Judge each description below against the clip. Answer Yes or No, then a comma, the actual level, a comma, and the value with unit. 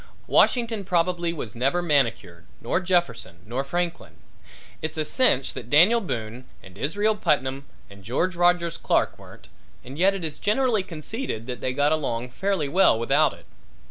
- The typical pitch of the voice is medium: Yes, medium, 155 Hz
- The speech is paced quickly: No, average, 160 wpm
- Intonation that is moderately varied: No, wide, 6.4 semitones